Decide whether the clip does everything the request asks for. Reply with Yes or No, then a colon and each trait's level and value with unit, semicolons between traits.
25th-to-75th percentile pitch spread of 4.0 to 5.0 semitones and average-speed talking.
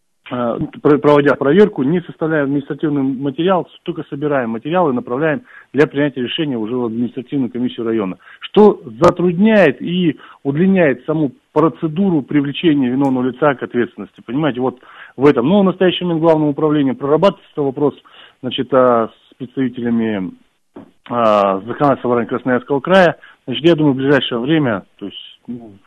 Yes: average, 4.6 semitones; average, 135 wpm